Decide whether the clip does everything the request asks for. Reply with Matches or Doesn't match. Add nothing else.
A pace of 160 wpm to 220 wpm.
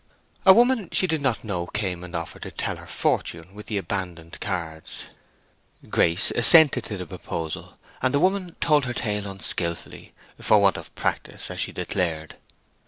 Matches